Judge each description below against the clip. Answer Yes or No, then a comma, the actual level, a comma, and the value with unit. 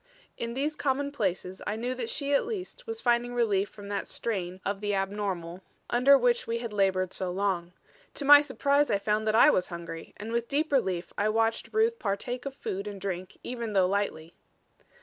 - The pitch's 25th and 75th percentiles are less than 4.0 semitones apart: No, average, 5.1 semitones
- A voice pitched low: No, high, 215 Hz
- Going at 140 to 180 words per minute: No, average, 195 wpm